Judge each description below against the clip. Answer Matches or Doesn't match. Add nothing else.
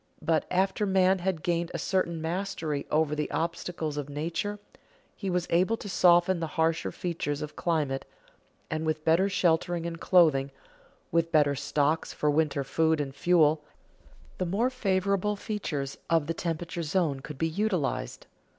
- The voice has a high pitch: Doesn't match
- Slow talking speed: Doesn't match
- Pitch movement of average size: Matches